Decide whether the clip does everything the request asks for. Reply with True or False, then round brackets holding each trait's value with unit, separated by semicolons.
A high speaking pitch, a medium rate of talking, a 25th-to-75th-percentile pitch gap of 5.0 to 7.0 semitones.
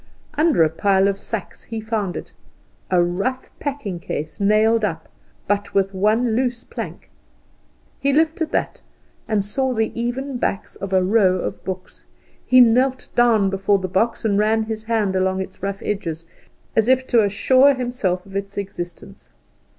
False (210 Hz; 165 wpm; 4.0 semitones)